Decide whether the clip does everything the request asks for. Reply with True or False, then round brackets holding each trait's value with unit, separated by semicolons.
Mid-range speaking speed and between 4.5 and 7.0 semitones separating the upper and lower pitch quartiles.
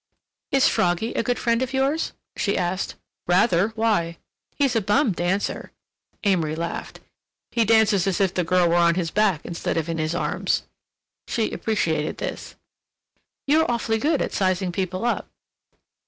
True (155 wpm; 4.9 semitones)